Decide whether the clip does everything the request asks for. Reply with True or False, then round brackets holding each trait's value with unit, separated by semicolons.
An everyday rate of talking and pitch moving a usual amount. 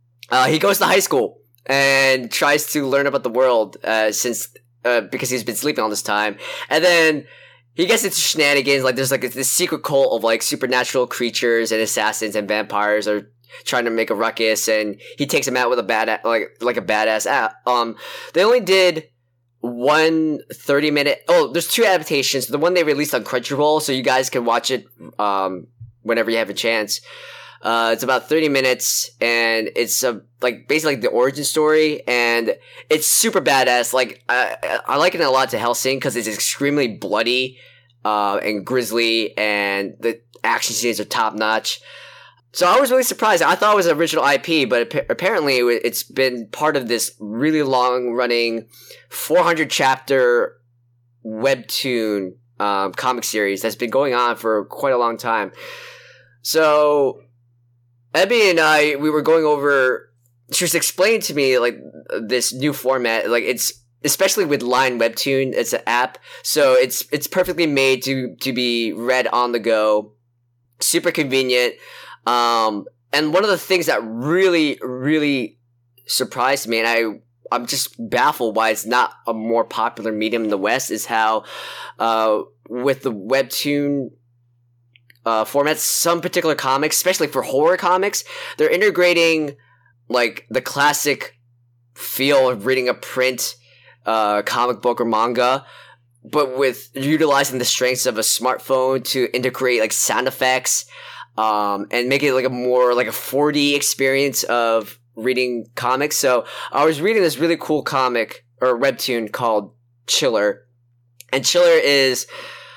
True (165 wpm; 3.7 semitones)